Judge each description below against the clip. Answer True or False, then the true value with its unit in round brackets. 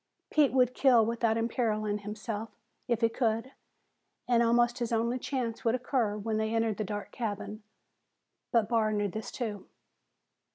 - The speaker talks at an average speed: True (155 wpm)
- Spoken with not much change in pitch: True (1.9 semitones)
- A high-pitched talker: True (230 Hz)